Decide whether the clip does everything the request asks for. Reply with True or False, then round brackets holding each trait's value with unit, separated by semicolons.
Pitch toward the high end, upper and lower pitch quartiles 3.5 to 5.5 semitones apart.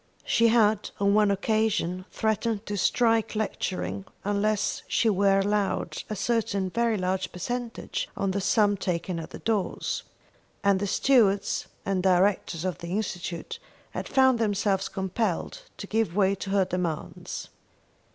False (200 Hz; 2.7 semitones)